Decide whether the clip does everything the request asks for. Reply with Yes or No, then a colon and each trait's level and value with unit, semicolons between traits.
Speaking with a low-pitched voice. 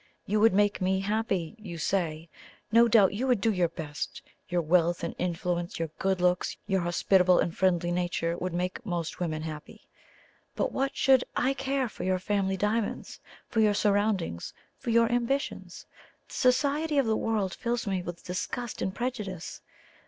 No: high, 190 Hz